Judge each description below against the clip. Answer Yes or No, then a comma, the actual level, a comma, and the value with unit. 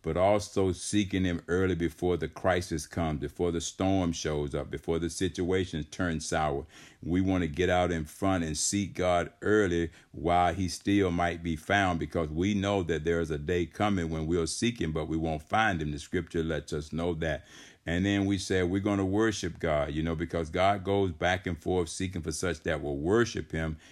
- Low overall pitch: Yes, very low, 85 Hz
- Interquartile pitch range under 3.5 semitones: Yes, average, 2.7 semitones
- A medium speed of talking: No, fast, 210 wpm